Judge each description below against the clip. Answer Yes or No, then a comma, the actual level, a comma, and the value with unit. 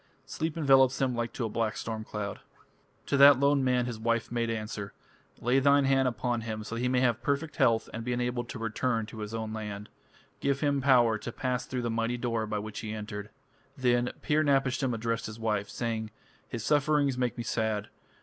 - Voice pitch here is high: No, low, 120 Hz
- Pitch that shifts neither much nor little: Yes, average, 3.0 semitones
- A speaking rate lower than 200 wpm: No, fast, 205 wpm